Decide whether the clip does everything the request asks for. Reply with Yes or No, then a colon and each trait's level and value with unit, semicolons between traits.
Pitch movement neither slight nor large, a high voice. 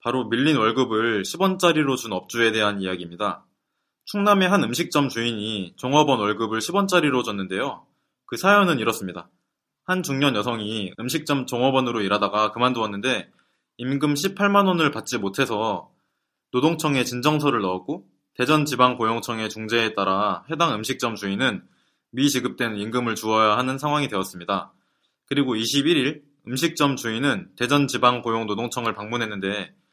No: average, 5.0 semitones; low, 125 Hz